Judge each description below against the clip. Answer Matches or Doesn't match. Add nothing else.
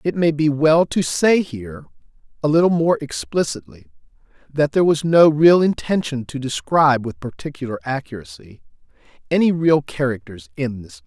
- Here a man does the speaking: Matches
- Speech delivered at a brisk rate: Doesn't match